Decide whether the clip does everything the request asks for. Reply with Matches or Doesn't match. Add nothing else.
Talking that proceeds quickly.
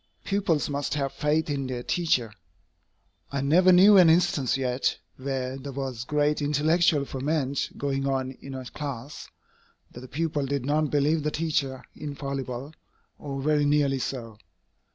Doesn't match